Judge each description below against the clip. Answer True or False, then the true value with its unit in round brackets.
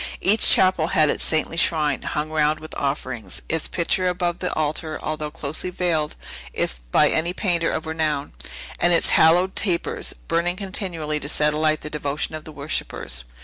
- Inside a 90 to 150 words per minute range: False (170 wpm)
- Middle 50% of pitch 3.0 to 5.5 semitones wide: False (2.5 semitones)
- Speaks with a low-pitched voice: False (155 Hz)